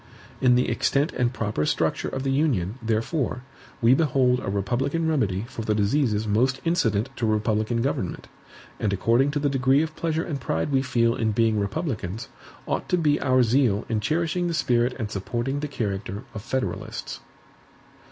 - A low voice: Yes, low, 125 Hz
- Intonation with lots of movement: No, average, 4.5 semitones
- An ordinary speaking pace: Yes, average, 170 wpm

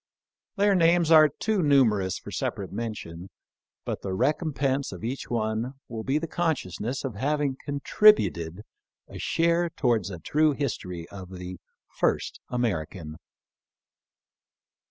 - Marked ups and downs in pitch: Yes, wide, 8.0 semitones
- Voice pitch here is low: Yes, low, 125 Hz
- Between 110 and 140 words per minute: Yes, slow, 135 wpm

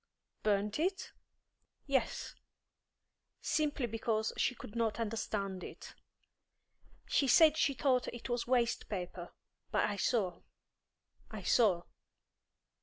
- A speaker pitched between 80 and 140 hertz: No, high, 230 Hz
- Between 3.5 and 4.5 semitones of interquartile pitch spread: Yes, average, 4.0 semitones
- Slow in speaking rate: Yes, slow, 110 wpm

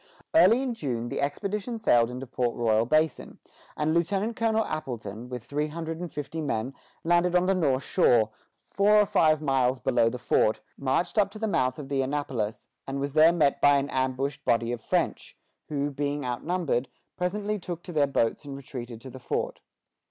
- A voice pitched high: No, medium, 145 Hz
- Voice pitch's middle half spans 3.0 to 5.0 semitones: No, wide, 5.5 semitones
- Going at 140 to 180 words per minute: No, average, 190 wpm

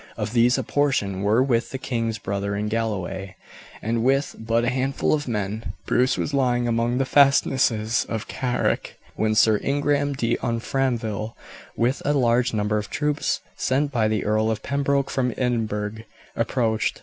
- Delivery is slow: No, average, 160 wpm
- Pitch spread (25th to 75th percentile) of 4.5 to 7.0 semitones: No, average, 3.6 semitones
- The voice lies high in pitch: No, low, 115 Hz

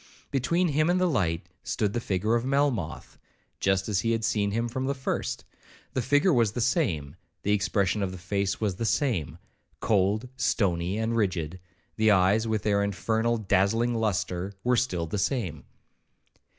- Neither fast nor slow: Yes, average, 170 wpm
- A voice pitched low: Yes, low, 105 Hz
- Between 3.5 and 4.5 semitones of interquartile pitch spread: Yes, average, 4.1 semitones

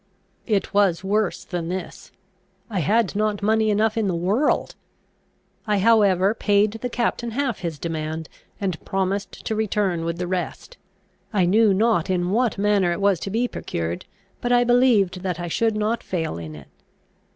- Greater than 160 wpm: Yes, average, 170 wpm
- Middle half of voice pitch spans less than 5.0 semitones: Yes, average, 3.8 semitones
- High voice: Yes, high, 200 Hz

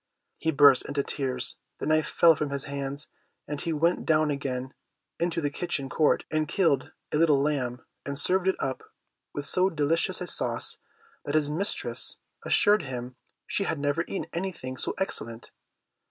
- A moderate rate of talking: Yes, average, 170 wpm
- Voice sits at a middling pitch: Yes, medium, 150 Hz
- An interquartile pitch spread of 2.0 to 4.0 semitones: Yes, average, 3.2 semitones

